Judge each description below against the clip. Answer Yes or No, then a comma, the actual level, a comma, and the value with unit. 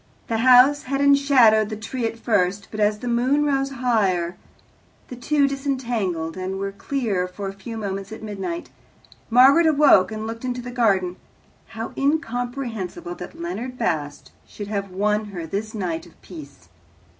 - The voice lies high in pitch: Yes, high, 225 Hz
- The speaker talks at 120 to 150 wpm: No, average, 160 wpm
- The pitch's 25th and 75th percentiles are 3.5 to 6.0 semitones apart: Yes, average, 5.1 semitones